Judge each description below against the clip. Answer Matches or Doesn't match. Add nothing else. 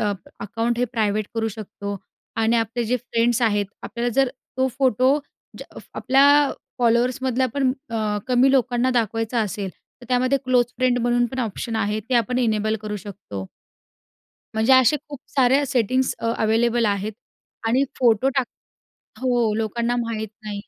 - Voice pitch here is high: Matches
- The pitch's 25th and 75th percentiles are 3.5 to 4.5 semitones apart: Doesn't match